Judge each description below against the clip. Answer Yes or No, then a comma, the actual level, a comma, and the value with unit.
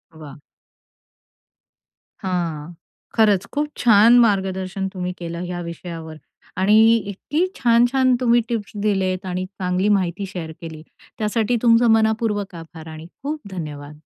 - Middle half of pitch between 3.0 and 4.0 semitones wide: No, average, 4.6 semitones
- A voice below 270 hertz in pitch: Yes, high, 190 Hz